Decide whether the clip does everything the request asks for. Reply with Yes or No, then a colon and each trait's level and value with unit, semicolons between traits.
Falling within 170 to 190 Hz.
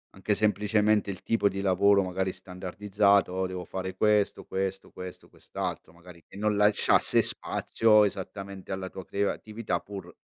No: low, 100 Hz